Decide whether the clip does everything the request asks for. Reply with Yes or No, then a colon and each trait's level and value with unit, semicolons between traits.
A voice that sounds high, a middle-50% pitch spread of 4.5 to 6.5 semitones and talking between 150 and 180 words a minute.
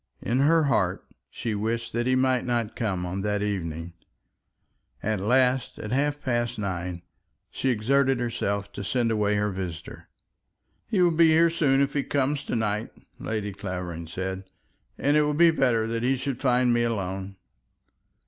No: low, 115 Hz; average, 5.1 semitones; average, 165 wpm